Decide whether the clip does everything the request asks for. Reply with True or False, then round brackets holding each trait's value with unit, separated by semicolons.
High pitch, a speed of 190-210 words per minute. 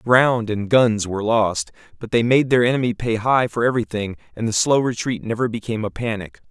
False (115 Hz; 205 wpm)